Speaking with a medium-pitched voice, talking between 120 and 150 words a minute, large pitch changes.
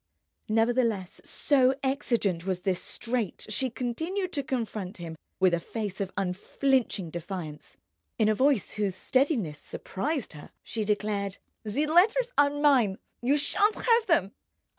No: high, 225 Hz; average, 140 wpm; wide, 6.5 semitones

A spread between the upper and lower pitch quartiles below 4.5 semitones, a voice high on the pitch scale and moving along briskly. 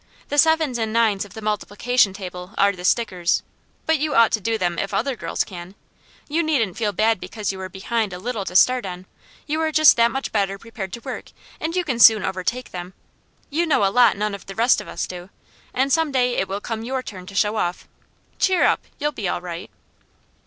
No: average, 4.8 semitones; high, 220 Hz; fast, 225 wpm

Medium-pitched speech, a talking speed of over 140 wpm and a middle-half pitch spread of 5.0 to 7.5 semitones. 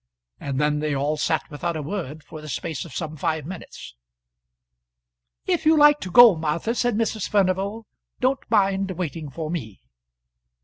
Yes: medium, 170 Hz; average, 165 wpm; wide, 5.6 semitones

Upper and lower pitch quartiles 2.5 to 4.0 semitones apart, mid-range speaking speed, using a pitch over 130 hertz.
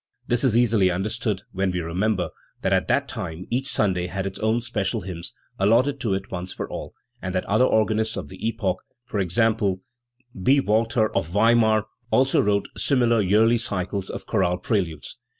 No: average, 3.6 semitones; average, 180 wpm; low, 105 Hz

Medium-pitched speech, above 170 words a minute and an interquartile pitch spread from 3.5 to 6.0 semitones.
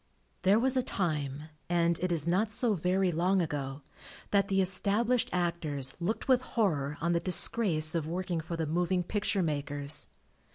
No: medium, 175 Hz; average, 165 wpm; average, 4.0 semitones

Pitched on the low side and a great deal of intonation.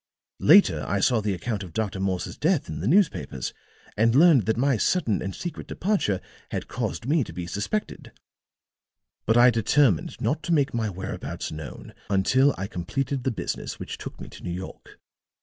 Yes: low, 110 Hz; wide, 6.9 semitones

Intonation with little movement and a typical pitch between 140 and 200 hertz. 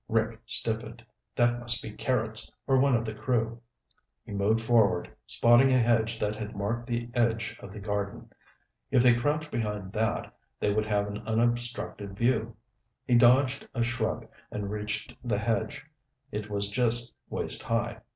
No: narrow, 2.3 semitones; low, 115 Hz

